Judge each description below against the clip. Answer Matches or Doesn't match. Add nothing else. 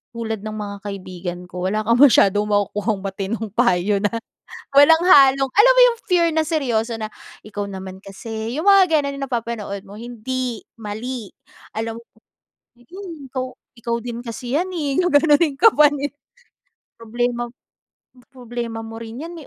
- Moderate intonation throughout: Matches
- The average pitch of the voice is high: Matches